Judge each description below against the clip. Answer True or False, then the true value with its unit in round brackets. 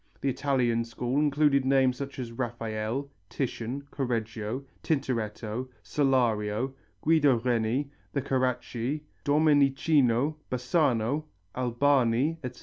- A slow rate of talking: True (95 wpm)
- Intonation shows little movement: False (3.3 semitones)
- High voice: False (130 Hz)